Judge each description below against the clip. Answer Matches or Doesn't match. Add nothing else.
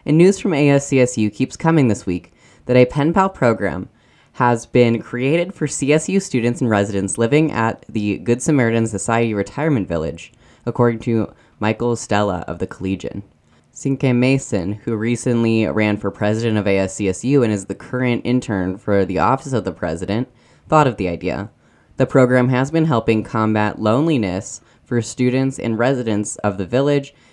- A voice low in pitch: Matches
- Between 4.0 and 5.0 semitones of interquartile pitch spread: Matches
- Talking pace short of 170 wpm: Matches